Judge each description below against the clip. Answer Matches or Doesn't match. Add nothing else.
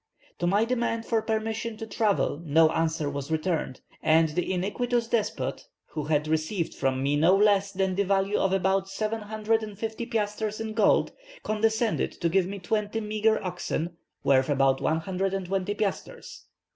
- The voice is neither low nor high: Doesn't match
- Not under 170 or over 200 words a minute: Doesn't match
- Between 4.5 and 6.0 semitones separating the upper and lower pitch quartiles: Matches